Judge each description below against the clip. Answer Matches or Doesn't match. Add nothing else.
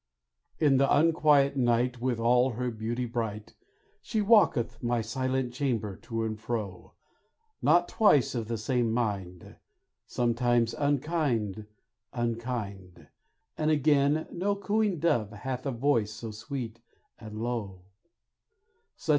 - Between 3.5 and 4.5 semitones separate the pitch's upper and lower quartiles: Matches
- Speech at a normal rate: Doesn't match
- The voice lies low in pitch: Matches